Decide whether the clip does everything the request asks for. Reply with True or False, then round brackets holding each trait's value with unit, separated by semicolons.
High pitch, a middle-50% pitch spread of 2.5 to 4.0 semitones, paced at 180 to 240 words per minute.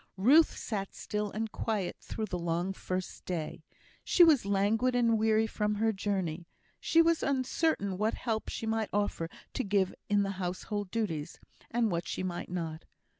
False (205 Hz; 3.4 semitones; 170 wpm)